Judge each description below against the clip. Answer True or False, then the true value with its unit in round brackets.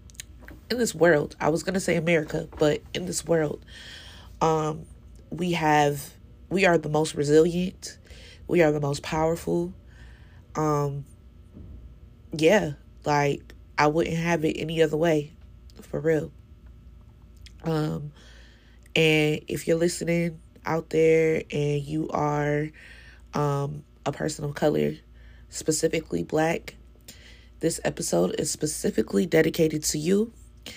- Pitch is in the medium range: True (155 Hz)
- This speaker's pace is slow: True (120 wpm)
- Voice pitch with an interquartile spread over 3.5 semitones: True (5.5 semitones)